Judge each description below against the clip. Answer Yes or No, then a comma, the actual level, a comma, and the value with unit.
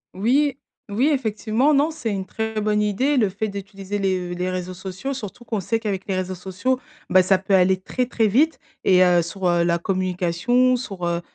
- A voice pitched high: Yes, high, 200 Hz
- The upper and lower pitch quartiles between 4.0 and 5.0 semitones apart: Yes, average, 4.3 semitones